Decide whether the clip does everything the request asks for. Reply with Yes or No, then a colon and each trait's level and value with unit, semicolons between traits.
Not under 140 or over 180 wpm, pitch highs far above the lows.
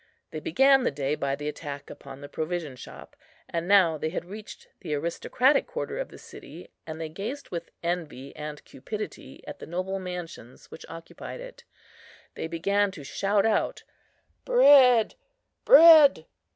Yes: average, 155 wpm; wide, 8.3 semitones